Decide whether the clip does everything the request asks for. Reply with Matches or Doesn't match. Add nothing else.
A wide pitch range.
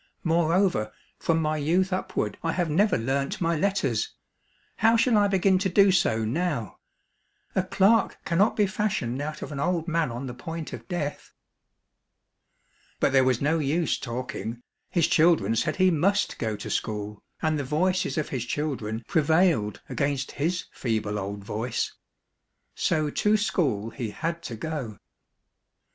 Matches